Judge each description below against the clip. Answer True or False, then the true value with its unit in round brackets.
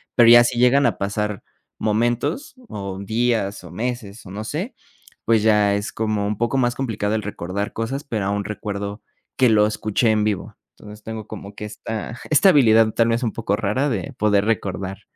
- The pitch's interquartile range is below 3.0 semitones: True (2.6 semitones)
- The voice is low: True (110 Hz)